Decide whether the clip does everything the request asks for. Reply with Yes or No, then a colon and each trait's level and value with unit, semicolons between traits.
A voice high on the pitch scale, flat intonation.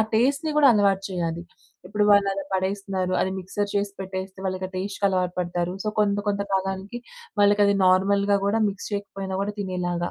Yes: high, 195 Hz; narrow, 1.5 semitones